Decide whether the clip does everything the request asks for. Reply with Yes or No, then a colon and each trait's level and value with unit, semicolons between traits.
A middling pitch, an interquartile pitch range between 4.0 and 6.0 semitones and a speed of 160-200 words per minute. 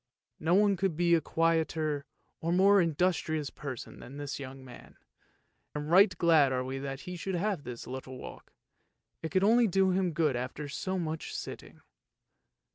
Yes: medium, 160 Hz; average, 4.8 semitones; average, 170 wpm